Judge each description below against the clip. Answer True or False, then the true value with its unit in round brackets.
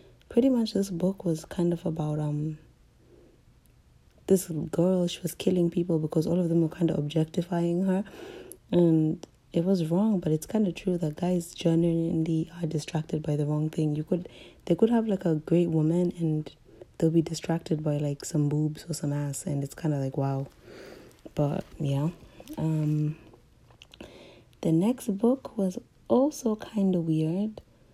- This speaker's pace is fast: False (170 wpm)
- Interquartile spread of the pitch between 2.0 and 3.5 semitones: True (2.9 semitones)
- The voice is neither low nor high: True (165 Hz)